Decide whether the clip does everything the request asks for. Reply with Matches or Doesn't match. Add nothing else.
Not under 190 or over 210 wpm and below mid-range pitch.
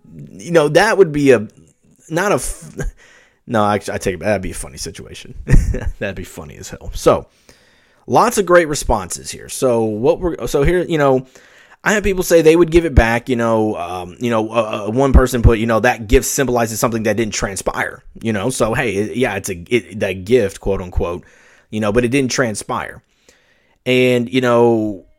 Matches